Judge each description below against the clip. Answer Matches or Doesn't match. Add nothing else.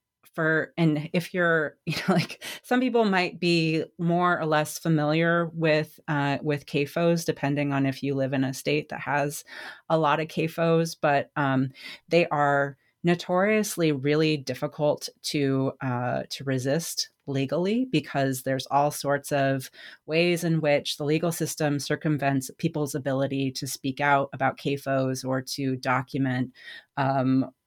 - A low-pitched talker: Doesn't match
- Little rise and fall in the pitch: Doesn't match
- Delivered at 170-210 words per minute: Doesn't match